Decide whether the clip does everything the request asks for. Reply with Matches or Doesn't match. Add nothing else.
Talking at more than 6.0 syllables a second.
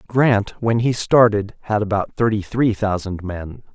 Doesn't match